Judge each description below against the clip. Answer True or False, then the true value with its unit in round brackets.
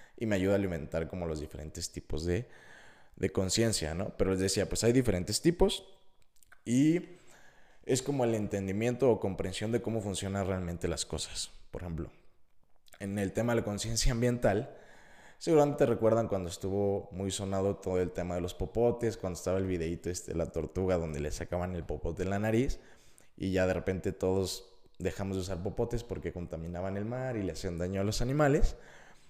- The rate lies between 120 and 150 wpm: False (185 wpm)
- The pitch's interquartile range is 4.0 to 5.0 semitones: True (4.3 semitones)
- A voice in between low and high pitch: False (95 Hz)